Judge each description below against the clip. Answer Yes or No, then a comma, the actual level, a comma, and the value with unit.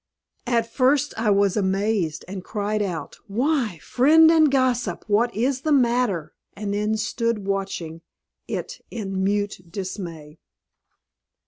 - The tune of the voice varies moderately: Yes, average, 4.2 semitones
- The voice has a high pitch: Yes, high, 210 Hz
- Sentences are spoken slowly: Yes, slow, 125 wpm